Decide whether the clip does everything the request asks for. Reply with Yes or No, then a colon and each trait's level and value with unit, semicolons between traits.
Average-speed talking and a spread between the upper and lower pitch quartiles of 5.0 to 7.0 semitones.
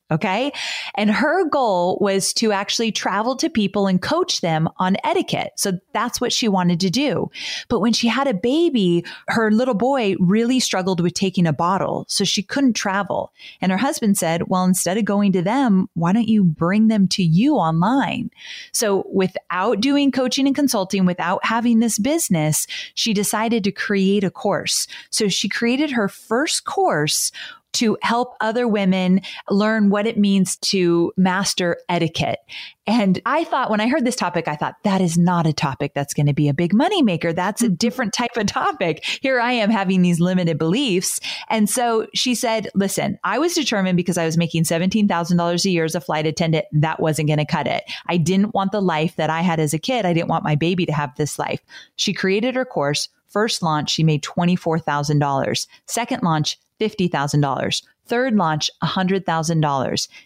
Yes: average, 185 wpm; average, 5.3 semitones